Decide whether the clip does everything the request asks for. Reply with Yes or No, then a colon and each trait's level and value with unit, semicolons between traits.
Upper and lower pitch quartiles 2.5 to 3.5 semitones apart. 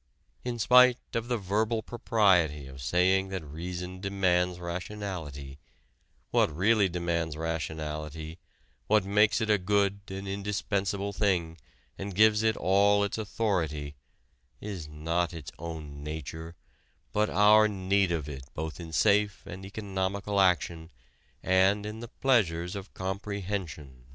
No: average, 3.9 semitones